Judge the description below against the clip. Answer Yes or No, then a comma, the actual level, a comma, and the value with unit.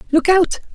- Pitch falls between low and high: No, very high, 350 Hz